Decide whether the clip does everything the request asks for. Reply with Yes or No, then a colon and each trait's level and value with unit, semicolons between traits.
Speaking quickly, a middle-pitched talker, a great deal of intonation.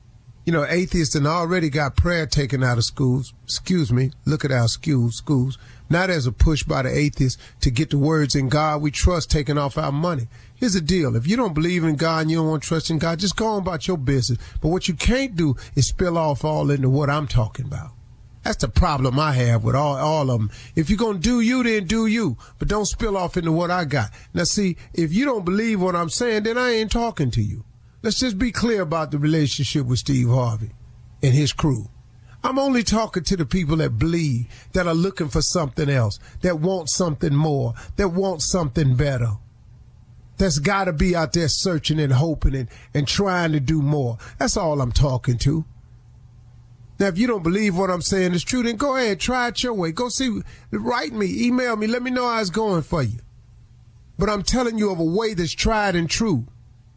Yes: fast, 225 wpm; medium, 155 Hz; wide, 6.8 semitones